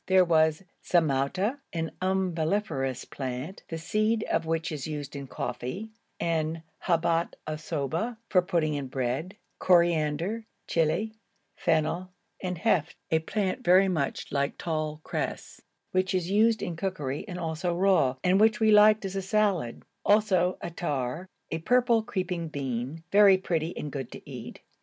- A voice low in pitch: No, medium, 170 Hz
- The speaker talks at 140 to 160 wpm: Yes, average, 145 wpm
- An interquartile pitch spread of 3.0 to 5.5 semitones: Yes, average, 4.0 semitones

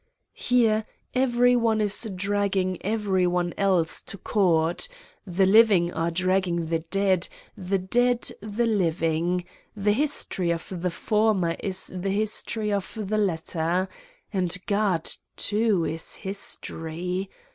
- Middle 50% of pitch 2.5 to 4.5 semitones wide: Yes, average, 3.4 semitones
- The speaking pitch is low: No, high, 190 Hz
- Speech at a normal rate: No, slow, 125 wpm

